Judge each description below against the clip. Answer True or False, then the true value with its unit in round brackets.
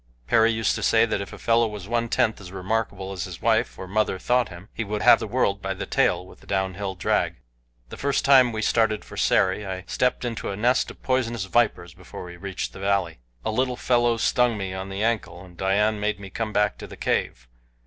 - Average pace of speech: False (235 wpm)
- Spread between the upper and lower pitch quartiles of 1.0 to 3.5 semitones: True (3.2 semitones)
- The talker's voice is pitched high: False (105 Hz)